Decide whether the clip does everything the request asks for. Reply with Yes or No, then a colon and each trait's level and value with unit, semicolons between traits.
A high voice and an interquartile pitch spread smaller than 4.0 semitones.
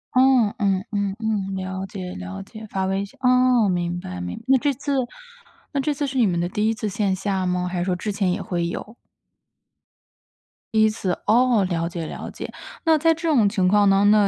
No: high, 200 Hz; average, 4.3 semitones